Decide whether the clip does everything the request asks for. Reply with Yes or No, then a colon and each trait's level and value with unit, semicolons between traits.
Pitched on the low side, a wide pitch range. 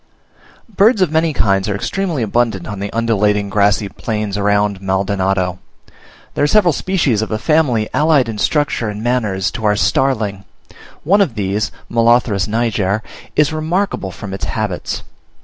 Yes: low, 110 Hz; wide, 6.3 semitones